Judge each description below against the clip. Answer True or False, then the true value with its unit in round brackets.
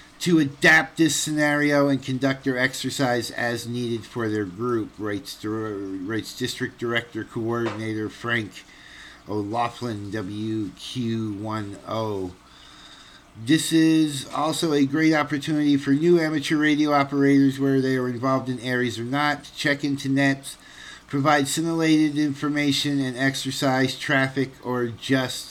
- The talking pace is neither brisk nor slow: False (120 wpm)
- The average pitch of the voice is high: False (135 Hz)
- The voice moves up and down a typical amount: True (3.9 semitones)